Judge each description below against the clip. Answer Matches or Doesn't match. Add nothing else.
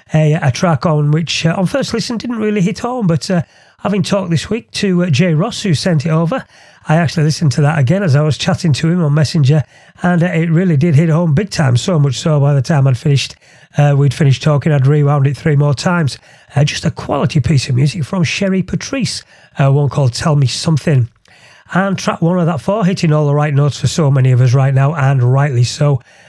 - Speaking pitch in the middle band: Matches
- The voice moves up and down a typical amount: Matches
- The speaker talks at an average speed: Doesn't match